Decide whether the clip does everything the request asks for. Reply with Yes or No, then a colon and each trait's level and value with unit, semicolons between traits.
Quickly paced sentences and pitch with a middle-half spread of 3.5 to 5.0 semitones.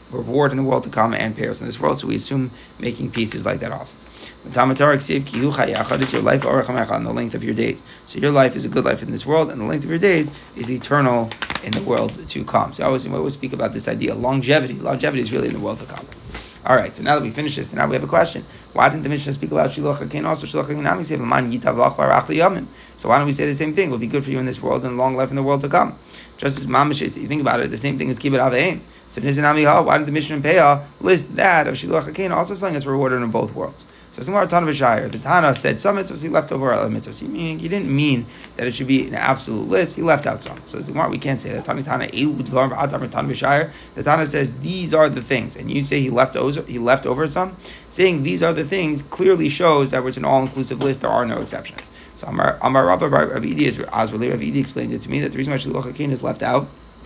No: fast, 250 wpm; average, 2.9 semitones